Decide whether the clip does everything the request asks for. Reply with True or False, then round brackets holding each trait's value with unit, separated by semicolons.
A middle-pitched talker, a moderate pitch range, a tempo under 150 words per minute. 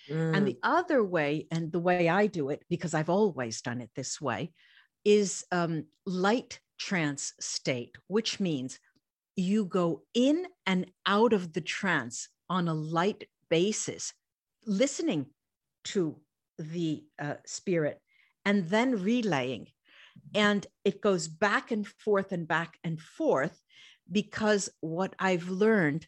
True (180 Hz; 4.8 semitones; 135 wpm)